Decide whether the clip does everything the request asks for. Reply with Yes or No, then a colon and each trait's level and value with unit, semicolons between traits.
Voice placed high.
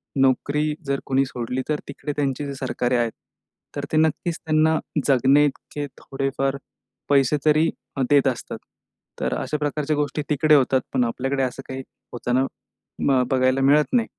No: medium, 140 Hz